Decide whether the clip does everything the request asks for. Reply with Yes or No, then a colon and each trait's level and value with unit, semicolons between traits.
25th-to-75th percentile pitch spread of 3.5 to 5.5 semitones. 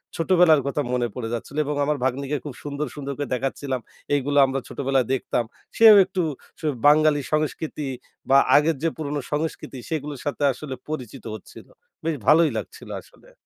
No: narrow, 2.4 semitones